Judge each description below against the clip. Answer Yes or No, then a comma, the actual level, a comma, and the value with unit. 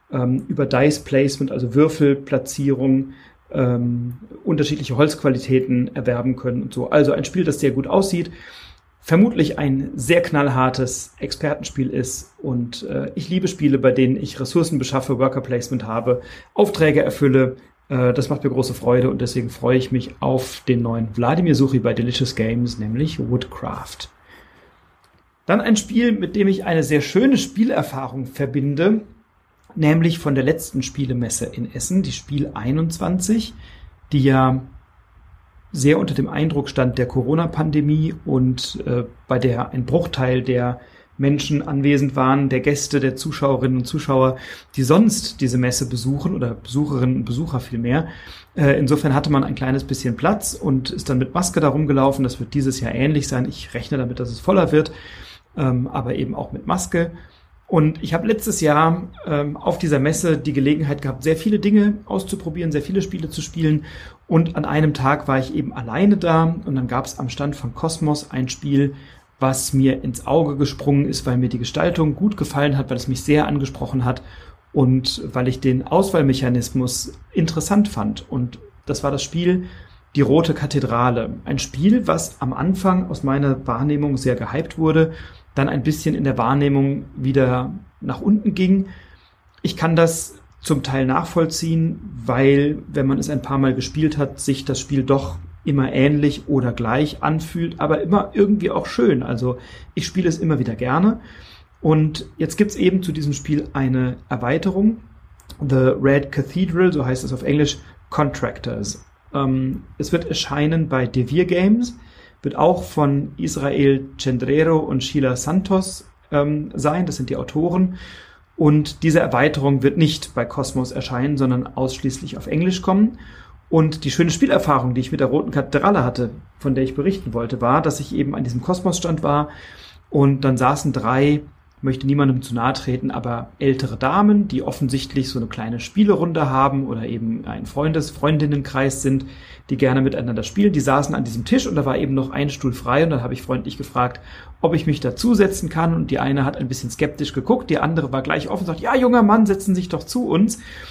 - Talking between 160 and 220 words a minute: Yes, average, 175 wpm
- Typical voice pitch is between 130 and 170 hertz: Yes, medium, 140 Hz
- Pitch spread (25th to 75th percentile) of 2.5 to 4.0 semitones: Yes, average, 3.6 semitones